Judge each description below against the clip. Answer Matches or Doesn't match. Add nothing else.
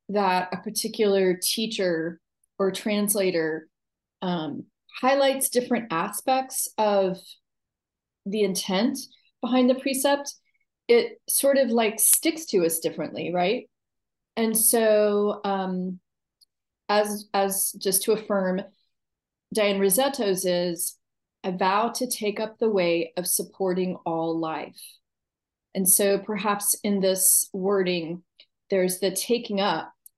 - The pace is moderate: Doesn't match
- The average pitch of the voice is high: Matches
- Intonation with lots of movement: Doesn't match